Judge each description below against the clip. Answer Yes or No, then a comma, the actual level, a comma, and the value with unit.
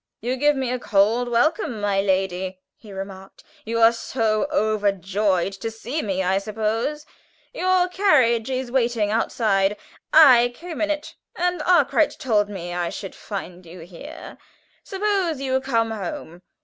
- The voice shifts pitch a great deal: Yes, wide, 5.8 semitones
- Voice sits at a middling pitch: No, high, 225 Hz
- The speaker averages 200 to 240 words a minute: No, average, 150 wpm